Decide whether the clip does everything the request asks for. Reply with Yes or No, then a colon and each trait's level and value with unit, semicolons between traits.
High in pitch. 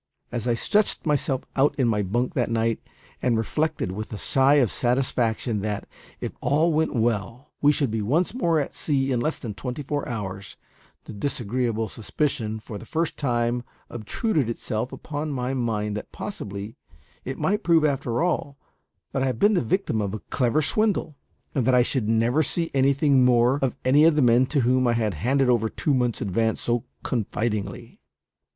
No: low, 125 Hz